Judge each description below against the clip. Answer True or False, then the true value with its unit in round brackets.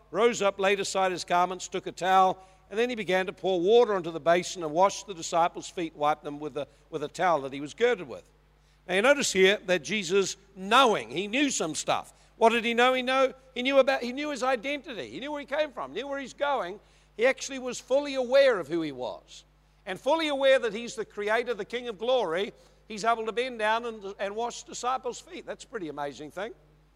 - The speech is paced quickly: True (235 wpm)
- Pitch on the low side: False (220 Hz)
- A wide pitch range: True (5.9 semitones)